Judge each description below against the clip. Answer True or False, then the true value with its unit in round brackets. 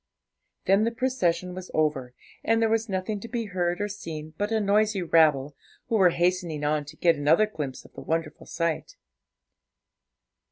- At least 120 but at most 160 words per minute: False (170 wpm)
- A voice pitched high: False (180 Hz)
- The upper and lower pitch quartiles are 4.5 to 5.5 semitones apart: True (5.2 semitones)